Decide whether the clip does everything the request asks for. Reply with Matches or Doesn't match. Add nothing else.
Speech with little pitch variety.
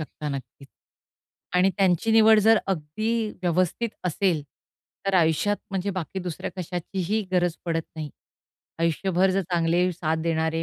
Doesn't match